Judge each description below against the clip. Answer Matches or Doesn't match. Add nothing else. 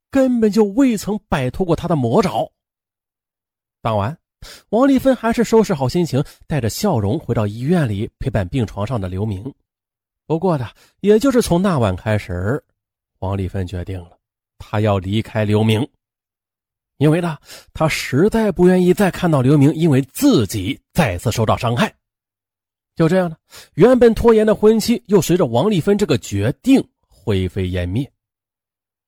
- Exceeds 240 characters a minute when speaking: Doesn't match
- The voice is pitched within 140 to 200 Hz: Doesn't match